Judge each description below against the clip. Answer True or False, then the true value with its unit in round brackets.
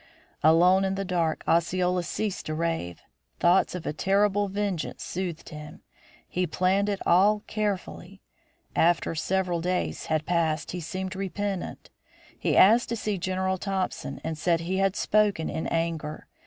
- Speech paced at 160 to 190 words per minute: False (150 wpm)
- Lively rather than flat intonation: False (2.8 semitones)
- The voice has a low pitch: False (185 Hz)